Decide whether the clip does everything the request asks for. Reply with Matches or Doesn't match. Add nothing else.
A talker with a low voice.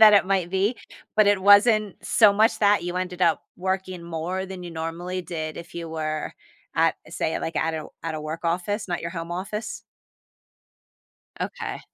Doesn't match